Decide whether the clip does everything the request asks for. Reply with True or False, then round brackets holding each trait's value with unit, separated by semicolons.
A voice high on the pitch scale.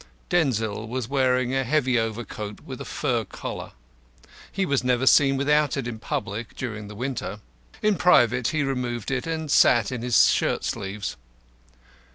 False (125 Hz)